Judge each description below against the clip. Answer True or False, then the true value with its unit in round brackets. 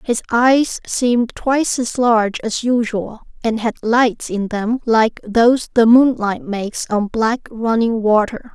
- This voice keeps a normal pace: True (155 wpm)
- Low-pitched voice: False (230 Hz)